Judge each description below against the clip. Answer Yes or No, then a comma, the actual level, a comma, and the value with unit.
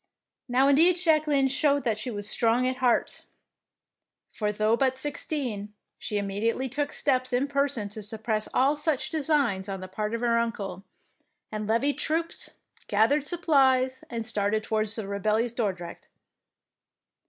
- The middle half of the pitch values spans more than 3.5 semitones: Yes, average, 4.7 semitones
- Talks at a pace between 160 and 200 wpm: No, average, 140 wpm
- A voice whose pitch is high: Yes, high, 240 Hz